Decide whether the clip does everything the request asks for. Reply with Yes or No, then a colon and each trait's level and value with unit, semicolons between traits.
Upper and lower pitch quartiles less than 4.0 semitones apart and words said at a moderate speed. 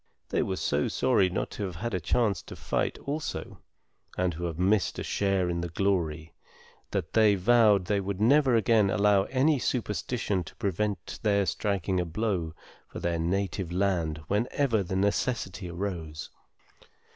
Yes: average, 3.6 semitones; average, 160 wpm